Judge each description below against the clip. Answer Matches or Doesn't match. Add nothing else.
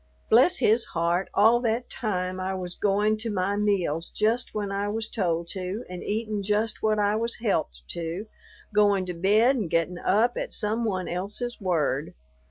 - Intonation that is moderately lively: Matches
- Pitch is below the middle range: Doesn't match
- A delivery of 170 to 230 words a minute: Matches